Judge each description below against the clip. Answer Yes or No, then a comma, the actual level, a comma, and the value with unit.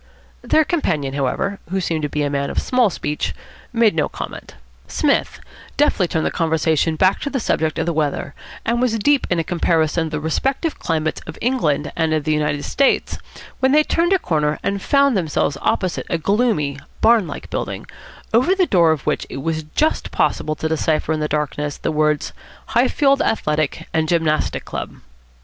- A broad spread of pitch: Yes, wide, 7.1 semitones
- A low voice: No, medium, 160 Hz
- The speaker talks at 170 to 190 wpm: Yes, average, 185 wpm